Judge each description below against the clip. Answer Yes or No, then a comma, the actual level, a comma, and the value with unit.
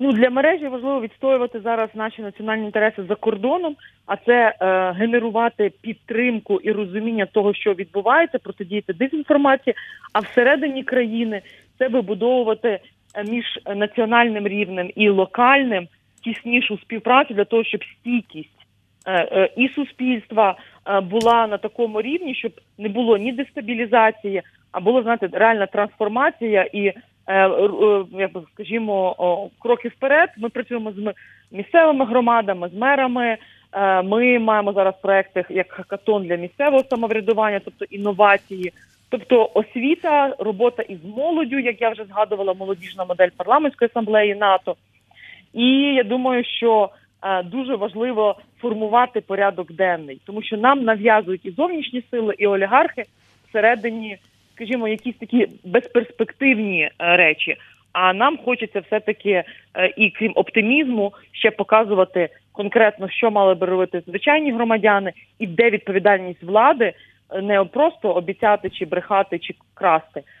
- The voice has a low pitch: No, high, 215 Hz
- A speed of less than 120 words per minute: No, average, 125 wpm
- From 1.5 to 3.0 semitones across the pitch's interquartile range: No, average, 3.7 semitones